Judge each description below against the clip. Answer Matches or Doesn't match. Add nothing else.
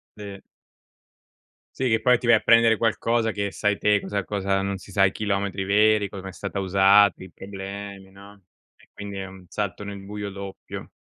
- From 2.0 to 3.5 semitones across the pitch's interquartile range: Doesn't match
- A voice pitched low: Matches